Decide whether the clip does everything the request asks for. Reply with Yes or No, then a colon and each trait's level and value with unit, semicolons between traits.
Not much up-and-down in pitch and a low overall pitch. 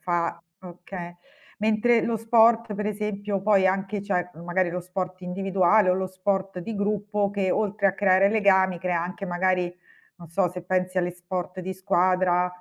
No: narrow, 2.1 semitones; high, 190 Hz